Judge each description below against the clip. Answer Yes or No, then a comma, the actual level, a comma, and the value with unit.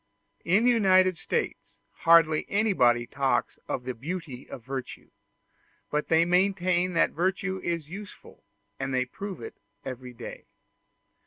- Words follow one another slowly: Yes, slow, 130 wpm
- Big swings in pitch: Yes, wide, 5.9 semitones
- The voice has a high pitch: No, medium, 170 Hz